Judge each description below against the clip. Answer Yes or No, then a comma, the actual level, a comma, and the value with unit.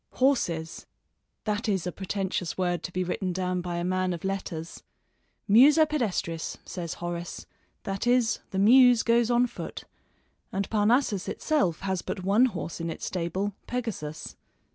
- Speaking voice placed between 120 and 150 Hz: No, high, 190 Hz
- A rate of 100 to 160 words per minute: Yes, average, 150 wpm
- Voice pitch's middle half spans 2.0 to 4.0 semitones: No, average, 4.9 semitones